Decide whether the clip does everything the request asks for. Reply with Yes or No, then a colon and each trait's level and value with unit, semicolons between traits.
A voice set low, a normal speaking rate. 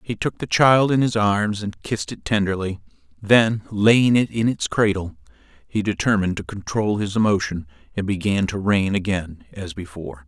Yes: low, 100 Hz; average, 175 wpm